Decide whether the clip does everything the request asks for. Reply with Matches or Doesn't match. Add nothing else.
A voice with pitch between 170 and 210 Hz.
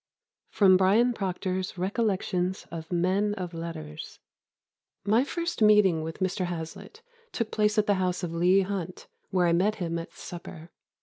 Matches